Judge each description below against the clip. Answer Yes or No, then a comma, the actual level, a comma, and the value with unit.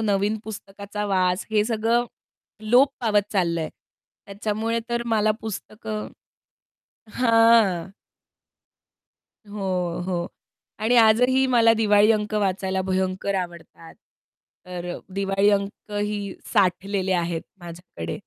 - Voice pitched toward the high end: Yes, high, 205 Hz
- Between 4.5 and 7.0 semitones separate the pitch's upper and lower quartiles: No, average, 2.8 semitones